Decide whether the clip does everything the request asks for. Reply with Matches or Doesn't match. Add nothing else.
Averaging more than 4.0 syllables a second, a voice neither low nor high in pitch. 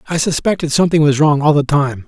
Matches